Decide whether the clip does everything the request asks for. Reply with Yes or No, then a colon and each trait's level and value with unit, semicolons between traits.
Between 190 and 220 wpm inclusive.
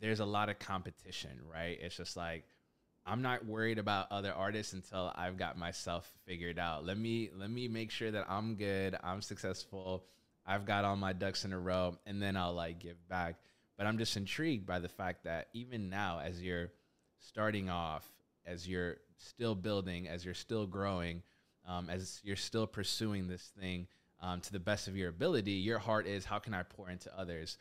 Yes: average, 200 wpm